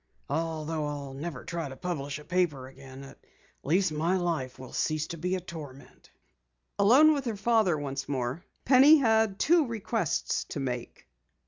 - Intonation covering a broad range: Yes, wide, 6.2 semitones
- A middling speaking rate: Yes, average, 160 wpm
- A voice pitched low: No, medium, 165 Hz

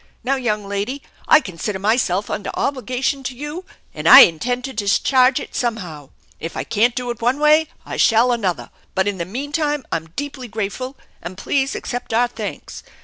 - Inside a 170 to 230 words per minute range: Yes, average, 180 wpm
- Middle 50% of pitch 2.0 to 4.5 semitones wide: No, average, 4.9 semitones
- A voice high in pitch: Yes, high, 240 Hz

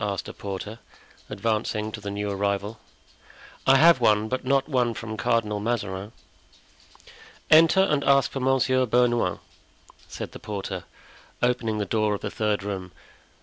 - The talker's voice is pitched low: Yes, low, 110 Hz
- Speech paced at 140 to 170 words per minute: Yes, average, 145 wpm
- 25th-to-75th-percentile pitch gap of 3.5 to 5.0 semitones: Yes, average, 3.8 semitones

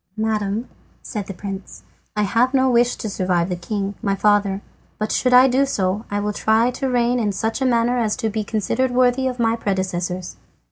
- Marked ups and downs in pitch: No, average, 3.7 semitones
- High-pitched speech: Yes, high, 220 Hz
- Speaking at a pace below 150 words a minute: No, average, 200 wpm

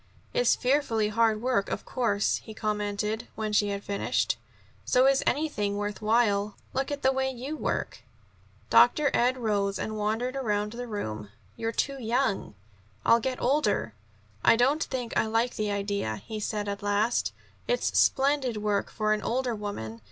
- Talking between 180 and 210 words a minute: No, average, 165 wpm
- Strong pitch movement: No, average, 3.7 semitones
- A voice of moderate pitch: No, high, 220 Hz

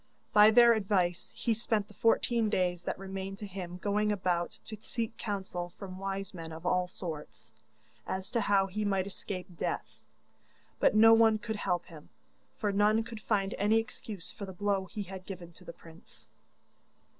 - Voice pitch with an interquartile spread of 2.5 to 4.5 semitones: Yes, average, 2.9 semitones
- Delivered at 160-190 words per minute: Yes, average, 180 wpm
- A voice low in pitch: No, high, 195 Hz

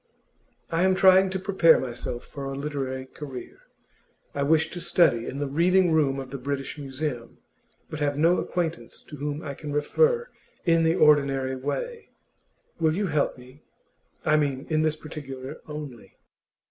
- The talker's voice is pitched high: No, medium, 150 Hz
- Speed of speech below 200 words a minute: Yes, average, 160 wpm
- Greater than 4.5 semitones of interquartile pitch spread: No, average, 3.4 semitones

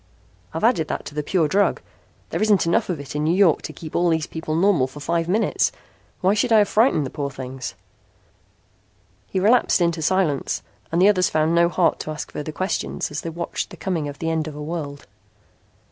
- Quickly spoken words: Yes, fast, 215 wpm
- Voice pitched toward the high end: No, medium, 165 Hz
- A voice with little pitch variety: No, average, 3.8 semitones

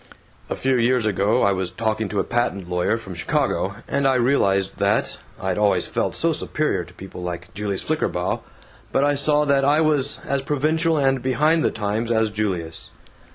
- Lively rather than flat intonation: Yes, wide, 6.1 semitones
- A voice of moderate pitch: No, low, 115 Hz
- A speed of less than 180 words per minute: No, average, 185 wpm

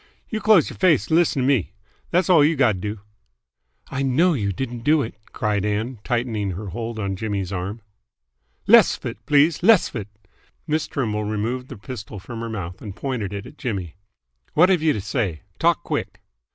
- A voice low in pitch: Yes, low, 115 Hz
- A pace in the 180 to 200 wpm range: Yes, average, 190 wpm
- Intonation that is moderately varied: No, wide, 6.0 semitones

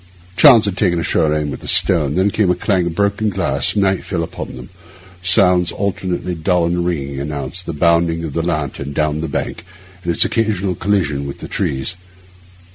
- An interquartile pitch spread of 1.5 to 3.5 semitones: No, average, 4.0 semitones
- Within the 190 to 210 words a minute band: Yes, average, 195 wpm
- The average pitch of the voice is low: Yes, very low, 85 Hz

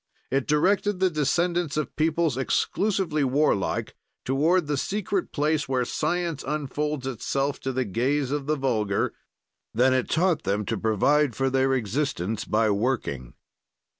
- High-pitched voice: No, medium, 140 Hz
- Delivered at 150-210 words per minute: No, average, 140 wpm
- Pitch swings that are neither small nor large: Yes, average, 3.5 semitones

